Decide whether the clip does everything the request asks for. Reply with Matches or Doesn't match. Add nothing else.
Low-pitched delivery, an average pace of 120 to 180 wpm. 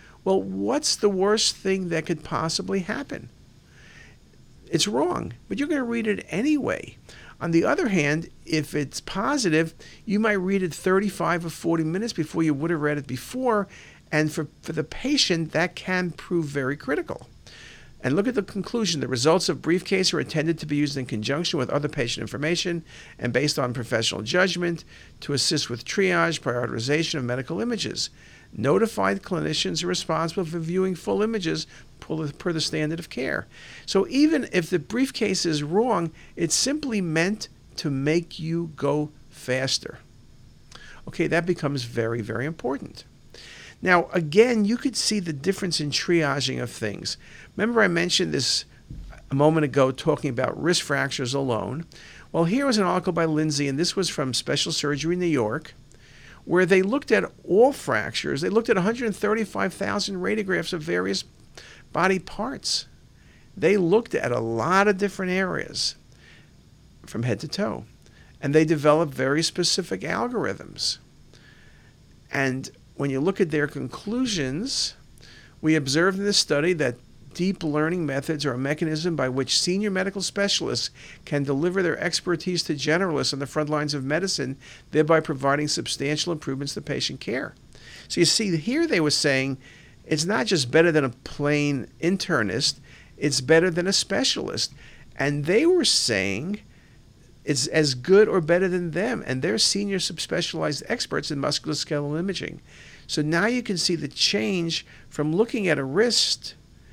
Doesn't match